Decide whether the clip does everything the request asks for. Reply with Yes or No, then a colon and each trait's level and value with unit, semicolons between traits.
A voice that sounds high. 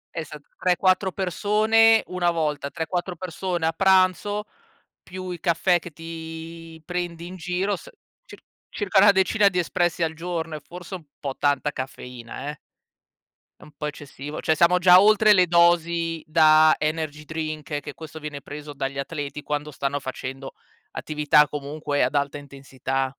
No: medium, 160 Hz